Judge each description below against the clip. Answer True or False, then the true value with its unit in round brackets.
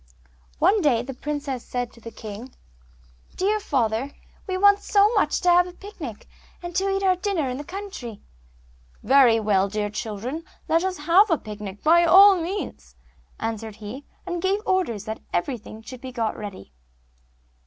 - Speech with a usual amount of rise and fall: False (8.9 semitones)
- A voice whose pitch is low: False (275 Hz)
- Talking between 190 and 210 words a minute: False (165 wpm)